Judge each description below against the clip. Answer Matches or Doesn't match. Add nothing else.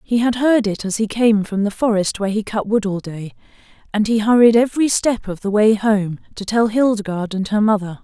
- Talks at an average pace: Doesn't match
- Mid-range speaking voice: Doesn't match